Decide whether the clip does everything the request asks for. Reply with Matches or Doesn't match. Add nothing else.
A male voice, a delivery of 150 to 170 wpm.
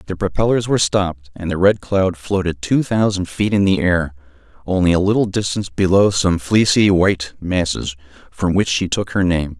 Doesn't match